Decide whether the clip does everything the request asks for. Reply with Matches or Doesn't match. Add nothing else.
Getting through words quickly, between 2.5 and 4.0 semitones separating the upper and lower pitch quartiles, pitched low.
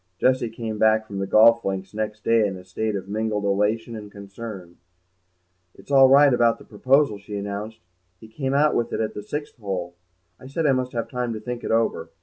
Matches